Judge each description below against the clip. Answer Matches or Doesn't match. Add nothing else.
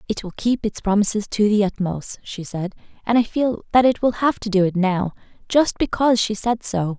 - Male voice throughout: Doesn't match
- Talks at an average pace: Doesn't match